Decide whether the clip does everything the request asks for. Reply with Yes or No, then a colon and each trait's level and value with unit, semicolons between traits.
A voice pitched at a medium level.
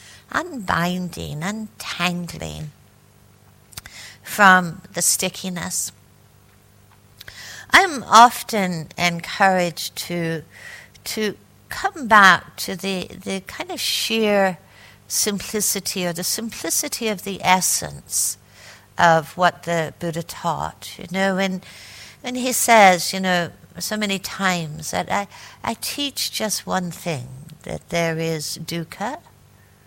Yes: medium, 175 Hz